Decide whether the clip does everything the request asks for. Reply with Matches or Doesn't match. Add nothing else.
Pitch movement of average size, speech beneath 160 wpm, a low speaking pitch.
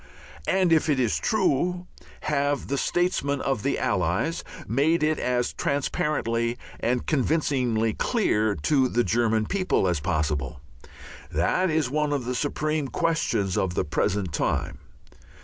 Doesn't match